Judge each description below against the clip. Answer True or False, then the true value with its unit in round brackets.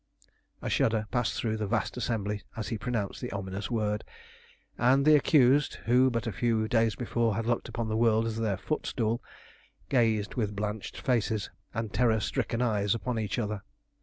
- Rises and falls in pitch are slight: True (2.3 semitones)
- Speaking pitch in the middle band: False (115 Hz)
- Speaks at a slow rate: False (175 wpm)